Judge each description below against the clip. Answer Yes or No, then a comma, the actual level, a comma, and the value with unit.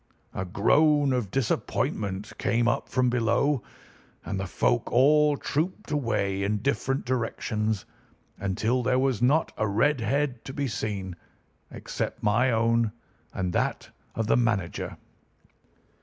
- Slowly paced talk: Yes, slow, 130 wpm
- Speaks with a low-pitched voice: Yes, low, 115 Hz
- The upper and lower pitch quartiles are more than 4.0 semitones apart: Yes, average, 4.5 semitones